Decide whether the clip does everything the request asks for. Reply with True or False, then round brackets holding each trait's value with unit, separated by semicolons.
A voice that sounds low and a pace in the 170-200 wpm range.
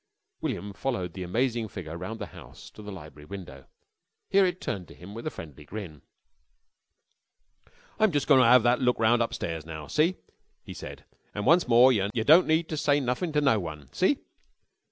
True (115 Hz; 195 wpm)